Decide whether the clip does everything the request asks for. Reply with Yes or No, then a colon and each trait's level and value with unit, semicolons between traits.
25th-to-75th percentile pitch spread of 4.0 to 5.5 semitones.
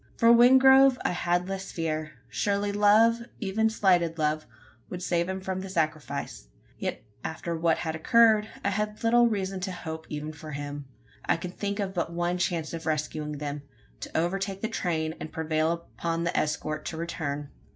Yes: average, 4.3 semitones